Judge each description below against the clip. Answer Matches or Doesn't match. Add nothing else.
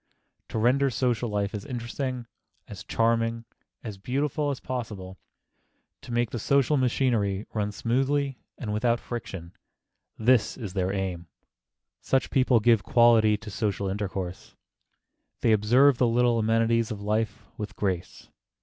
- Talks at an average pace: Doesn't match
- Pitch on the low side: Matches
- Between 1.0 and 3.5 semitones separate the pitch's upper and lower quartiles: Matches